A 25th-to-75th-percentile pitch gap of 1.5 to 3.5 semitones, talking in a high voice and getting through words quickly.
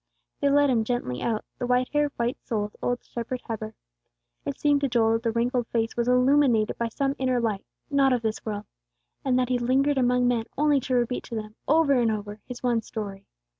Yes: average, 2.7 semitones; high, 245 Hz; fast, 210 wpm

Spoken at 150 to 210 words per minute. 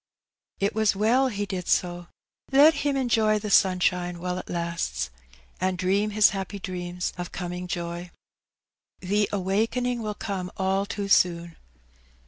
No: average, 140 wpm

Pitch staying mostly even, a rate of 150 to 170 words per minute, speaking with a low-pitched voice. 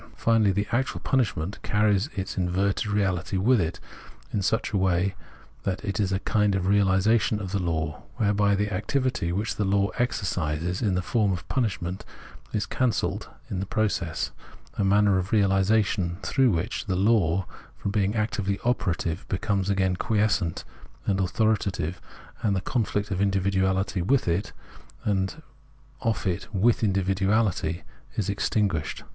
Yes: narrow, 2.3 semitones; average, 155 wpm; low, 100 Hz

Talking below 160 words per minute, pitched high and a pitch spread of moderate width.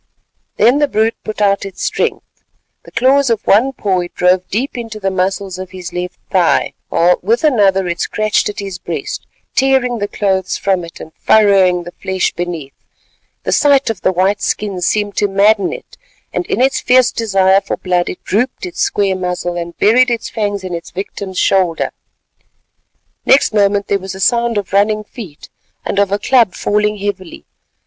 No: average, 185 wpm; high, 200 Hz; average, 3.1 semitones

